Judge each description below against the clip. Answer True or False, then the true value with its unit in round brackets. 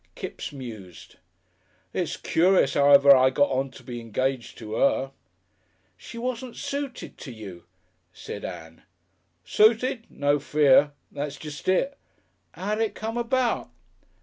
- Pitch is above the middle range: False (145 Hz)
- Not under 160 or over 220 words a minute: False (135 wpm)